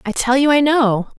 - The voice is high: Yes, very high, 255 Hz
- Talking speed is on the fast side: Yes, fast, 250 wpm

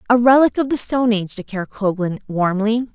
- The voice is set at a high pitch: Yes, high, 220 Hz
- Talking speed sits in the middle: Yes, average, 185 wpm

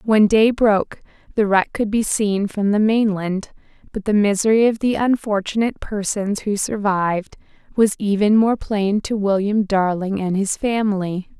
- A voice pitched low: No, high, 205 Hz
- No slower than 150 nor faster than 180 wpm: Yes, average, 160 wpm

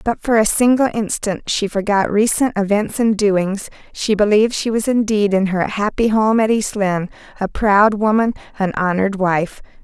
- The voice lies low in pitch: No, high, 210 Hz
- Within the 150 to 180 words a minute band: Yes, average, 175 wpm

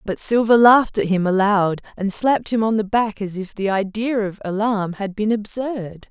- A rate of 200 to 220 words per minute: Yes, fast, 205 wpm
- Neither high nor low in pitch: No, high, 210 Hz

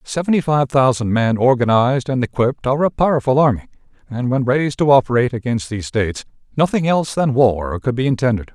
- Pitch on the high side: No, low, 130 Hz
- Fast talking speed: No, average, 180 wpm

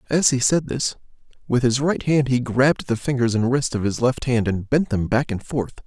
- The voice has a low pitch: Yes, low, 125 Hz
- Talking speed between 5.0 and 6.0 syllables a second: Yes, 5.2 syllables/s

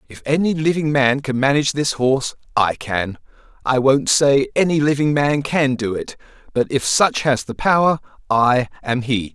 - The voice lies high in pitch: No, low, 135 Hz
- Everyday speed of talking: Yes, average, 175 wpm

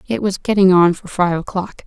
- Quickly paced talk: Yes, fast, 225 wpm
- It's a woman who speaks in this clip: Yes, female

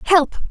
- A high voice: Yes, very high, 330 Hz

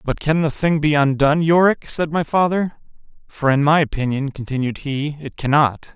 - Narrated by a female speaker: No, male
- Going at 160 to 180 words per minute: Yes, average, 170 wpm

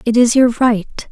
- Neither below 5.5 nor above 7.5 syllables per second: No, 5.0 syllables/s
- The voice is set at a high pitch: Yes, high, 235 Hz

